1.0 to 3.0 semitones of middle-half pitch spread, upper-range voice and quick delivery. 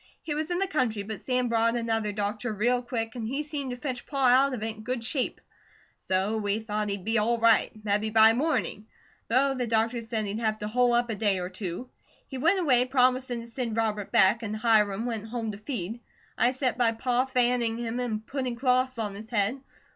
Yes: narrow, 2.6 semitones; high, 230 Hz; fast, 220 wpm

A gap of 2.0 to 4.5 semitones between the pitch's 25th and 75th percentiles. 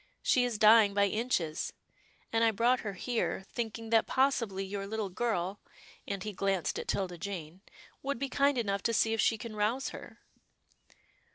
Yes: average, 3.0 semitones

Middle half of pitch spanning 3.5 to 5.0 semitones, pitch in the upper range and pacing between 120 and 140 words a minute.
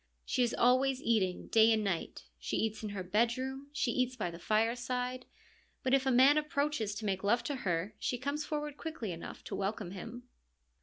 No: average, 4.3 semitones; high, 235 Hz; average, 195 wpm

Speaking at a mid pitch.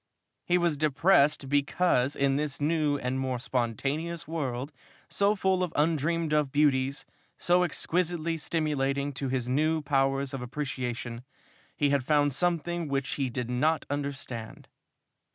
Yes: medium, 145 Hz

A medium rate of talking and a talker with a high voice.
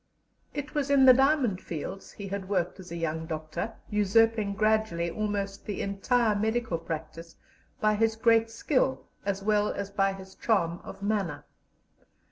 Yes: average, 155 wpm; high, 205 Hz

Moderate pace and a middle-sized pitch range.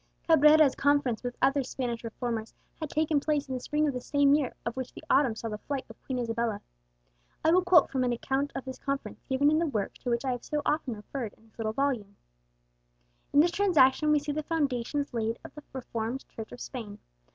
No: fast, 220 wpm; average, 3.8 semitones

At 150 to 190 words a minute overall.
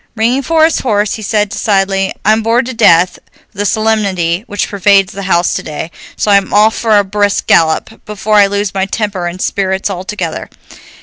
Yes: average, 185 wpm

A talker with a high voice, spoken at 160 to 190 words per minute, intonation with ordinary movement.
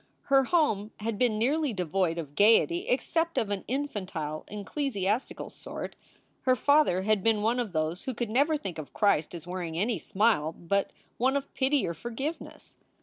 No: high, 215 Hz; average, 170 wpm; wide, 6.5 semitones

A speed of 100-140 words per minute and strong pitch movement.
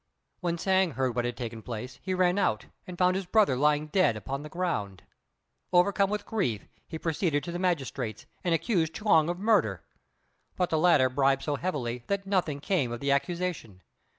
No: average, 185 wpm; wide, 6.1 semitones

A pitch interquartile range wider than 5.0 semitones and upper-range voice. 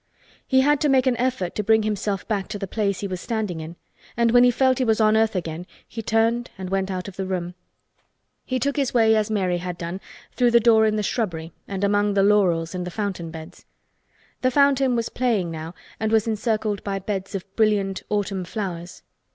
No: average, 3.6 semitones; high, 210 Hz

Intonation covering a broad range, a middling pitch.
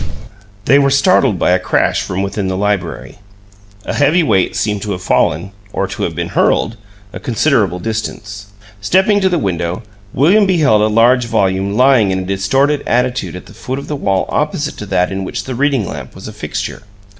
No: wide, 6.3 semitones; low, 105 Hz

